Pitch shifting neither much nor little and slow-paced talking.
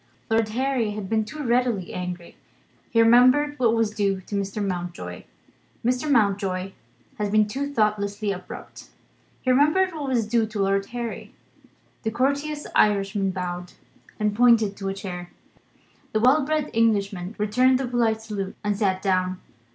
No: average, 4.0 semitones; average, 150 wpm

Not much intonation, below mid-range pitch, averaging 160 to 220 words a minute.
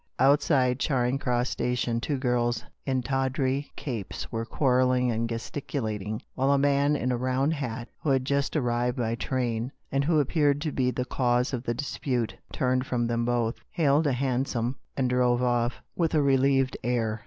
Yes: narrow, 2.3 semitones; low, 125 Hz; average, 175 wpm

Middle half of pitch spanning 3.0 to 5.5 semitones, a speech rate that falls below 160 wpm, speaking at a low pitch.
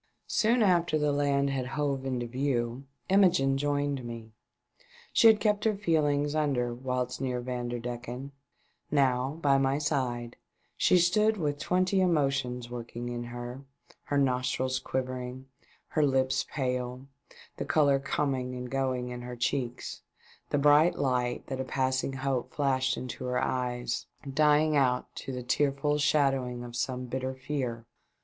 No: narrow, 2.6 semitones; average, 145 wpm; low, 130 Hz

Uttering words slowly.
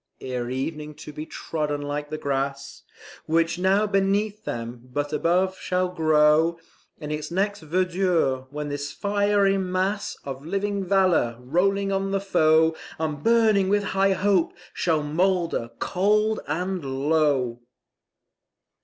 Yes: slow, 130 wpm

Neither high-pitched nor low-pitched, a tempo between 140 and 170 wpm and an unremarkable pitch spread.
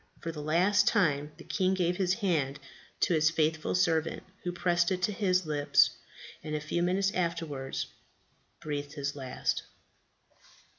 Yes: medium, 165 Hz; average, 150 wpm; average, 3.5 semitones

